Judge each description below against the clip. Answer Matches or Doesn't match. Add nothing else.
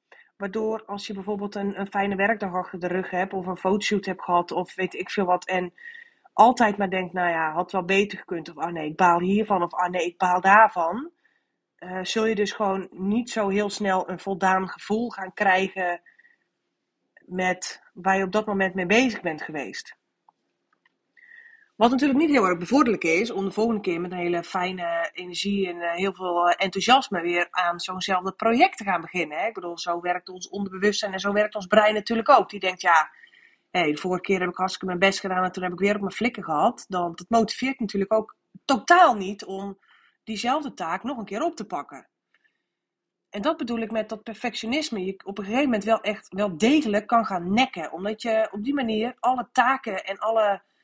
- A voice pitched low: Doesn't match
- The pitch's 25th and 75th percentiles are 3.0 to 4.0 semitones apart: Matches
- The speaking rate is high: Matches